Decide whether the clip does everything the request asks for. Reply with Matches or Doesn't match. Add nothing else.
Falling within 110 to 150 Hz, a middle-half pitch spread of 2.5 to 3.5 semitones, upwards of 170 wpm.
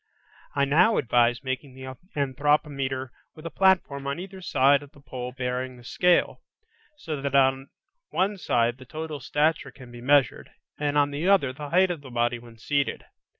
Matches